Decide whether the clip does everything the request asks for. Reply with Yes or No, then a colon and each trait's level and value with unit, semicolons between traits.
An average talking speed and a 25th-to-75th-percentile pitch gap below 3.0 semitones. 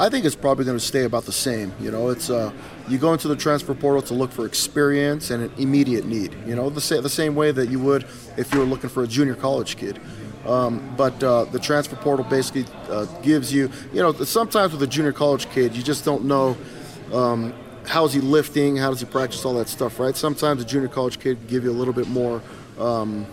No: fast, 245 wpm; narrow, 2.6 semitones